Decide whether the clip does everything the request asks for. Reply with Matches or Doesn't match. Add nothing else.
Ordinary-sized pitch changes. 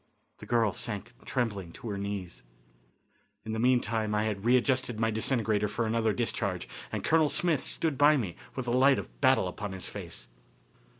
Matches